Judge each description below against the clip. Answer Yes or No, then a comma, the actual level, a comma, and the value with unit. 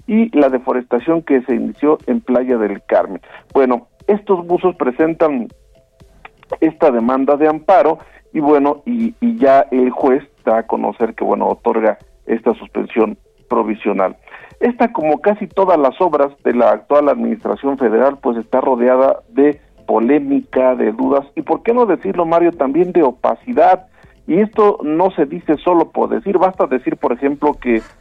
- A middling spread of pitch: No, wide, 6.1 semitones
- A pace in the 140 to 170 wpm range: Yes, average, 160 wpm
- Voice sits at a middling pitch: Yes, medium, 145 Hz